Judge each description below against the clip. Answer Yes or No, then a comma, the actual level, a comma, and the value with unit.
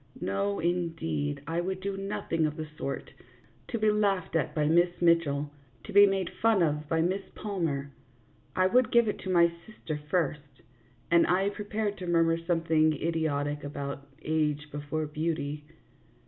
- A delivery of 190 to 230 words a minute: No, average, 160 wpm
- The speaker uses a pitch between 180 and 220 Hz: No, medium, 165 Hz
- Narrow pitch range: No, average, 3.9 semitones